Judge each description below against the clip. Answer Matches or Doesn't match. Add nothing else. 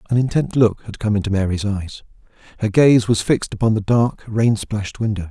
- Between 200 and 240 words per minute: Matches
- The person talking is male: Matches